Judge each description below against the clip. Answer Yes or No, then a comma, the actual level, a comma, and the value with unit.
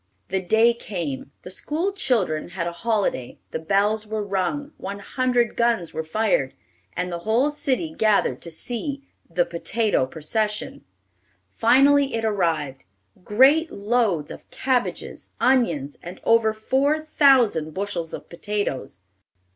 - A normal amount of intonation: No, wide, 6.3 semitones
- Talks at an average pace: No, slow, 130 wpm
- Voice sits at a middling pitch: No, high, 215 Hz